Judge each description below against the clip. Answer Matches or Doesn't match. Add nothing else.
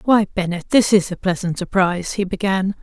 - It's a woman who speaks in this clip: Matches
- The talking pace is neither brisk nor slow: Matches